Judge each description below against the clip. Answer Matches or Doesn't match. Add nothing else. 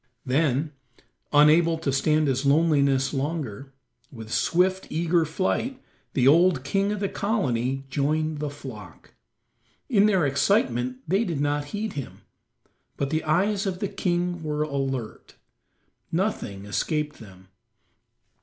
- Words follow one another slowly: Matches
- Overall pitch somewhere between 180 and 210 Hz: Doesn't match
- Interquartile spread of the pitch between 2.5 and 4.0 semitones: Doesn't match